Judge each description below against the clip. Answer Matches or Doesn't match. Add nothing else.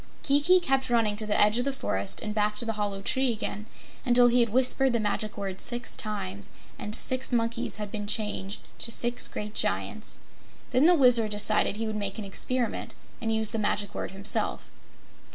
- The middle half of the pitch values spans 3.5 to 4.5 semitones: Doesn't match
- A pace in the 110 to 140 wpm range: Doesn't match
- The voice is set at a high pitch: Matches